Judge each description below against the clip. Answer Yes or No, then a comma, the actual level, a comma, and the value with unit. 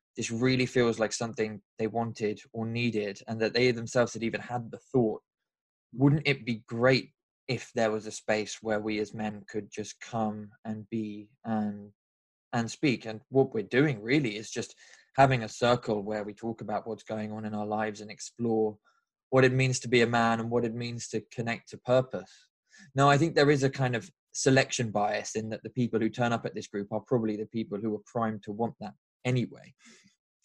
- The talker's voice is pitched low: Yes, low, 115 Hz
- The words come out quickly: Yes, fast, 210 wpm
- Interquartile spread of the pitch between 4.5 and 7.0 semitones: No, narrow, 2.5 semitones